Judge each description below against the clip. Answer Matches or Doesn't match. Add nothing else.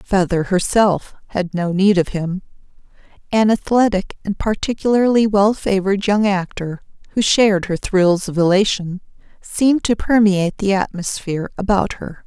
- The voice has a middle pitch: Doesn't match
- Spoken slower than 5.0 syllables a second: Matches